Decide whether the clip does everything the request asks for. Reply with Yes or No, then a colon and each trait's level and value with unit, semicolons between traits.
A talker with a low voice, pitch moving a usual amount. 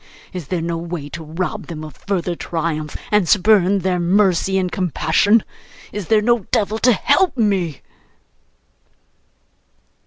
No: medium, 185 Hz; average, 3.8 semitones